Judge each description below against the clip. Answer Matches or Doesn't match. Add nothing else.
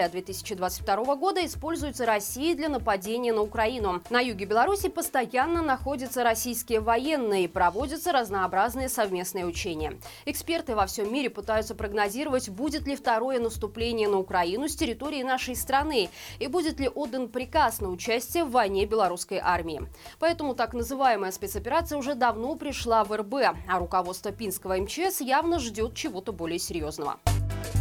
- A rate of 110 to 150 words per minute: Matches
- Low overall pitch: Doesn't match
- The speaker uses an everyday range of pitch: Doesn't match